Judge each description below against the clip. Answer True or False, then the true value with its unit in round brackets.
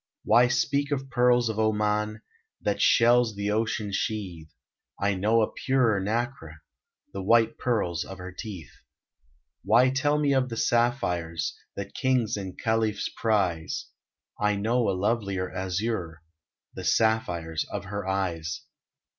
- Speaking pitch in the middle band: False (105 Hz)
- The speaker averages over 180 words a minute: False (135 wpm)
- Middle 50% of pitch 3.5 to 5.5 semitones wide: True (4.1 semitones)